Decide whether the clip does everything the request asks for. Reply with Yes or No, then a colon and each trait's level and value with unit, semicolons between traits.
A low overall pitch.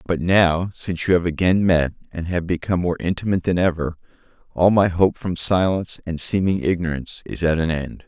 Yes: very low, 85 Hz